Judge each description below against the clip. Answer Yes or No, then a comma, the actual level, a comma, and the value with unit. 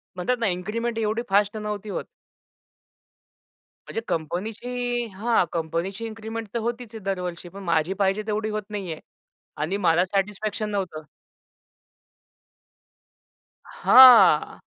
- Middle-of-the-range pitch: No, high, 210 Hz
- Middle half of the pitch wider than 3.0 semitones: Yes, average, 3.7 semitones